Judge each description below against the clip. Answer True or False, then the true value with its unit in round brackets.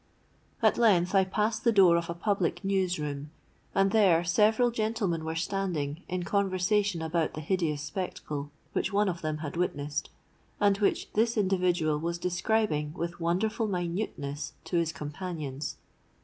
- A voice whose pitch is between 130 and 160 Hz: False (175 Hz)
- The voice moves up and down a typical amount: True (4.0 semitones)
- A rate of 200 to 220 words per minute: False (150 wpm)